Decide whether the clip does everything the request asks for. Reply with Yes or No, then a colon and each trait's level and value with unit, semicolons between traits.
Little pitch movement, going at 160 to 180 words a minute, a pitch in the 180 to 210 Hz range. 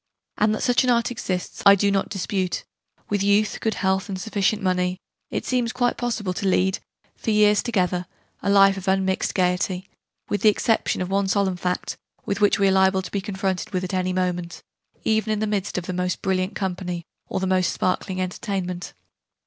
No: narrow, 2.2 semitones; average, 195 wpm; high, 190 Hz